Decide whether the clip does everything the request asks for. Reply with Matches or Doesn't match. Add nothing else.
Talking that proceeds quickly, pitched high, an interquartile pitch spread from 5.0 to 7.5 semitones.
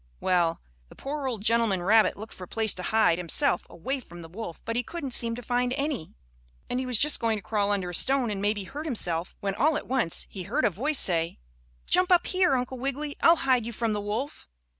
Matches